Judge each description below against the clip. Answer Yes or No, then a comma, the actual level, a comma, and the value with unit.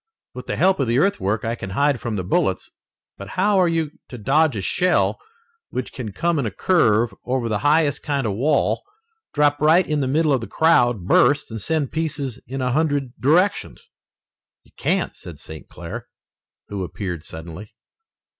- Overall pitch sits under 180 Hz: Yes, low, 135 Hz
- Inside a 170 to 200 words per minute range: Yes, average, 185 wpm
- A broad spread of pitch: Yes, wide, 6.2 semitones